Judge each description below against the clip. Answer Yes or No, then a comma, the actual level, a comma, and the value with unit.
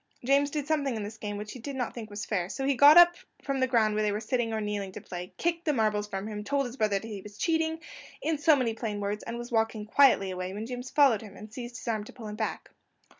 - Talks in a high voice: Yes, high, 225 Hz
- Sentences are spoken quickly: Yes, fast, 275 wpm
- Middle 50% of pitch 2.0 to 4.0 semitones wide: No, average, 4.6 semitones